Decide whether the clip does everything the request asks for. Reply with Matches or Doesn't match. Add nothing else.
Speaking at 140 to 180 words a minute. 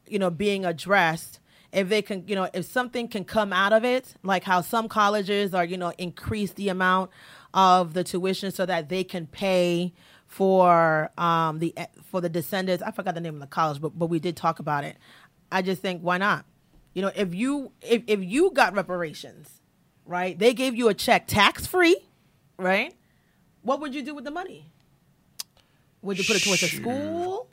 Doesn't match